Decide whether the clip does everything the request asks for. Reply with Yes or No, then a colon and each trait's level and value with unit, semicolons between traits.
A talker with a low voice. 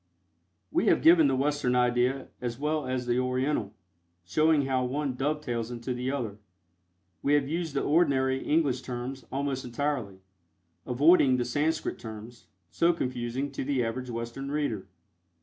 Yes: low, 130 Hz